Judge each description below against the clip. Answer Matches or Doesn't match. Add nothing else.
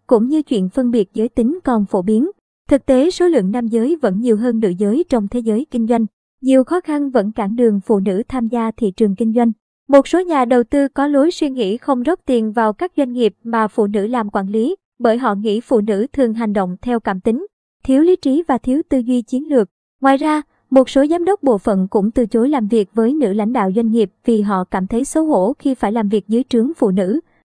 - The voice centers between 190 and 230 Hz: Doesn't match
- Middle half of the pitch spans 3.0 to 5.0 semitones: Matches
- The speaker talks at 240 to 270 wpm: Matches